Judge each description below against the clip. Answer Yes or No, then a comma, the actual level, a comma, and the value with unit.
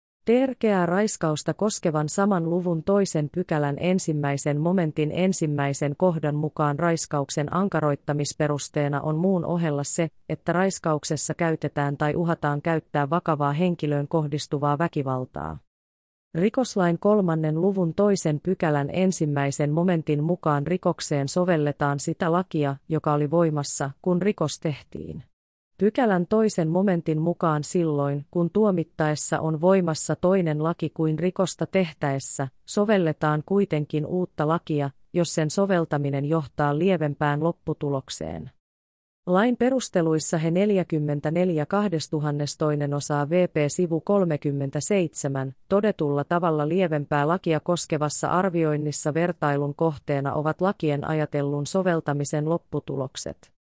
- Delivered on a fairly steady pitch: No, average, 3.3 semitones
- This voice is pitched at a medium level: Yes, medium, 160 Hz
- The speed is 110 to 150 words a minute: No, average, 100 wpm